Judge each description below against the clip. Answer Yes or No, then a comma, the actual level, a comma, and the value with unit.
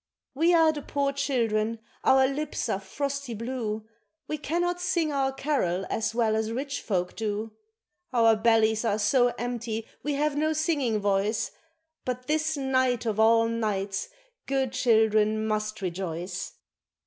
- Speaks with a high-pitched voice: Yes, high, 235 Hz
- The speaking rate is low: No, average, 145 wpm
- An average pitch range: Yes, average, 4.5 semitones